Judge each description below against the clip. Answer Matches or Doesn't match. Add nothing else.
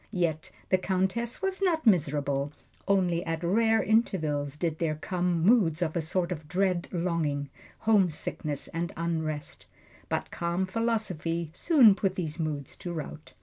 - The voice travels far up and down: Doesn't match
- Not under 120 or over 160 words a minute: Matches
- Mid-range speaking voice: Matches